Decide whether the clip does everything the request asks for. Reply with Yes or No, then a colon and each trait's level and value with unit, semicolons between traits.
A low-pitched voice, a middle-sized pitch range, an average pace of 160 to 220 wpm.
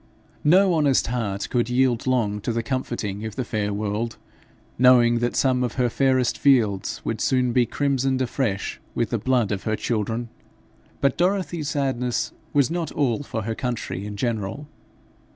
Yes: low, 125 Hz; average, 3.3 semitones; average, 165 wpm